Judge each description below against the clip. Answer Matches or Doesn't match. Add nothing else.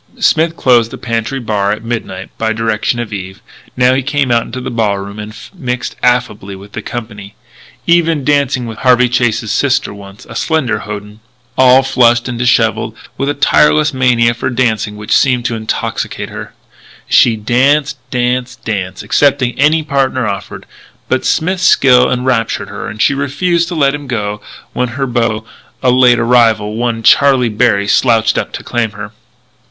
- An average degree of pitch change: Matches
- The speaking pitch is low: Matches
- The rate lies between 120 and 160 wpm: Doesn't match